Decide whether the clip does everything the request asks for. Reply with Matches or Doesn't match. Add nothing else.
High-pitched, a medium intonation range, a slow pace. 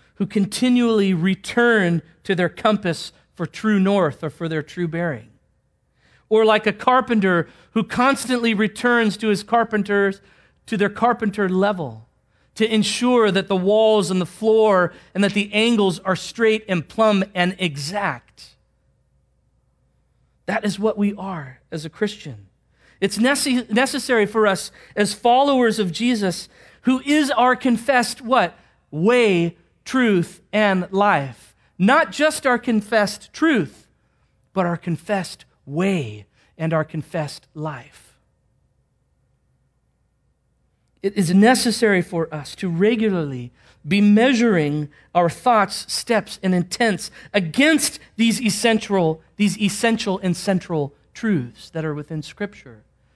Matches